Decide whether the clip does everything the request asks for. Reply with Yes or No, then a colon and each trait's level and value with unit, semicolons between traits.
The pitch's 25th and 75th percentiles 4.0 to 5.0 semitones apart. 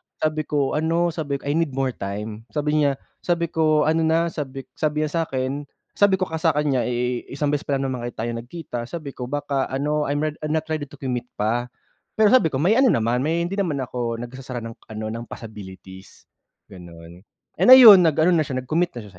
Yes: average, 4.6 semitones